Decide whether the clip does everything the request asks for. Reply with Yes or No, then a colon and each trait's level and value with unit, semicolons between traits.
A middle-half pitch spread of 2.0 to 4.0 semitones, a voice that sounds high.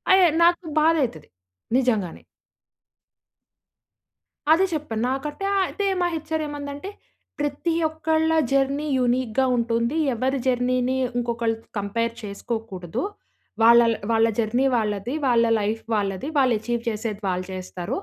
No: average, 4.6 semitones; high, 240 Hz